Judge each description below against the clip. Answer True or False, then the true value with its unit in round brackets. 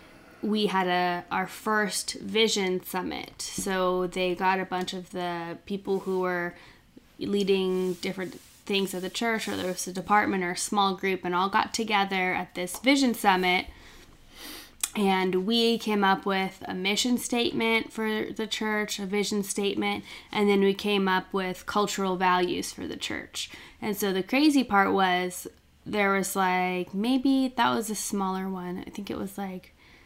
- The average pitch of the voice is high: True (195 Hz)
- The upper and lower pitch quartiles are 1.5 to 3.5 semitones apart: True (2.4 semitones)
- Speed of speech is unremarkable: True (170 wpm)